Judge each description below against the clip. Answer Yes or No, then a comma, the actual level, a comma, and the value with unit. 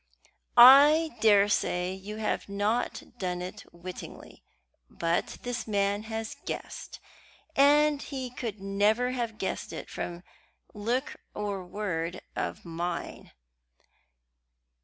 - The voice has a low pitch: No, high, 210 Hz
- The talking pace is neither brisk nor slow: No, slow, 105 wpm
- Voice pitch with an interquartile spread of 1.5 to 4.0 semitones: No, average, 4.8 semitones